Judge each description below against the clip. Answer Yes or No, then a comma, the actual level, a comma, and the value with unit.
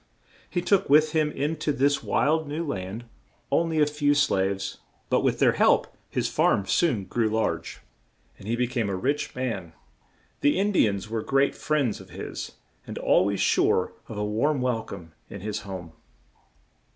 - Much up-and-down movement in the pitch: Yes, wide, 6.8 semitones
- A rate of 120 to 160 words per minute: No, average, 185 wpm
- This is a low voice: Yes, low, 125 Hz